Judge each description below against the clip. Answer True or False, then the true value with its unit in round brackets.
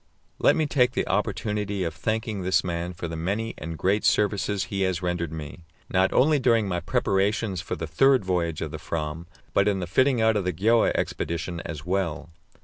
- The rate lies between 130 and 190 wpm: False (200 wpm)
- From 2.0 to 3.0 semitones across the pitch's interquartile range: False (3.9 semitones)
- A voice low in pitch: True (95 Hz)